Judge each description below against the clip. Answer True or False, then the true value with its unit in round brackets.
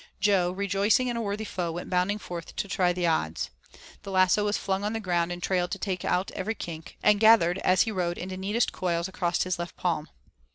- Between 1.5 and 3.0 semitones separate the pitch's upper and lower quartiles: True (2.6 semitones)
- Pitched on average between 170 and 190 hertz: True (185 Hz)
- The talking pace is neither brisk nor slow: False (220 wpm)